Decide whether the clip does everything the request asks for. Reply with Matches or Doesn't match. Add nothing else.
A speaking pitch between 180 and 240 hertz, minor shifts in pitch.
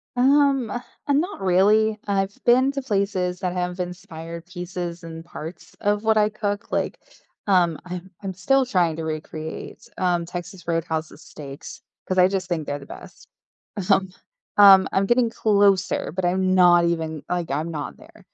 Doesn't match